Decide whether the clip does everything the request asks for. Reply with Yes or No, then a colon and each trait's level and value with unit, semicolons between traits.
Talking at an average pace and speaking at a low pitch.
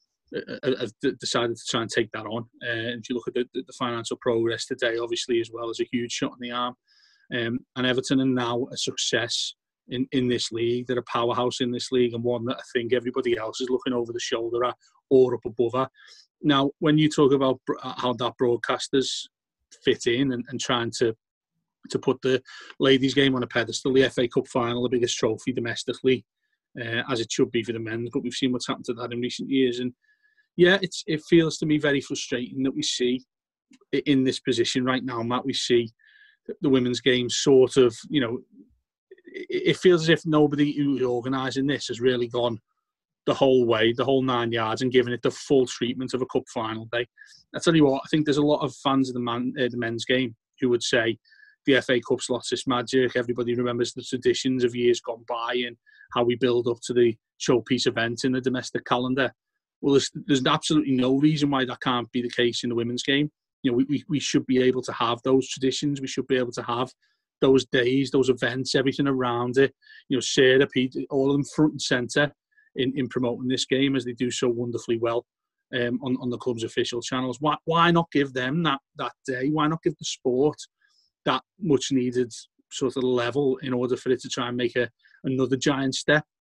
No: fast, 220 wpm; low, 130 Hz